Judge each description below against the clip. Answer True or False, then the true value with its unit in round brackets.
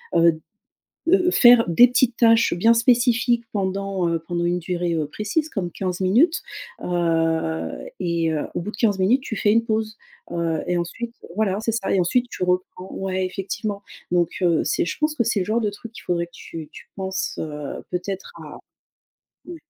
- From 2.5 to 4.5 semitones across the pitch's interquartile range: False (5.0 semitones)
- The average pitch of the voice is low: False (190 Hz)